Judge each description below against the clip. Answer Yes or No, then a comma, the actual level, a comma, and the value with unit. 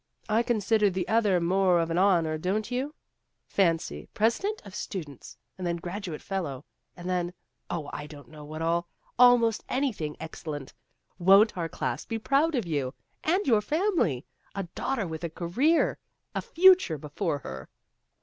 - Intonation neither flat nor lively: No, wide, 6.0 semitones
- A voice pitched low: No, medium, 185 Hz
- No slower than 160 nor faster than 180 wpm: Yes, average, 165 wpm